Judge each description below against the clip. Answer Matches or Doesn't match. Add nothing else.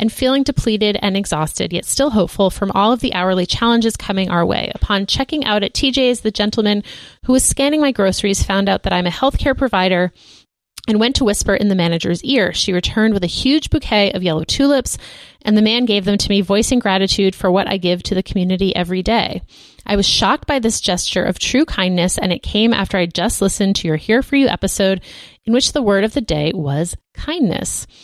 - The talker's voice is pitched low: Doesn't match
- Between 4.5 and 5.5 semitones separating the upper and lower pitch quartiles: Doesn't match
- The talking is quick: Matches